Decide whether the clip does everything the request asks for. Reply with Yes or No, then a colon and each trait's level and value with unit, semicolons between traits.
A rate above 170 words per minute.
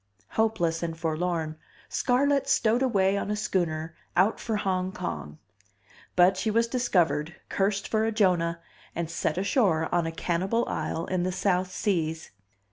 No: average, 150 wpm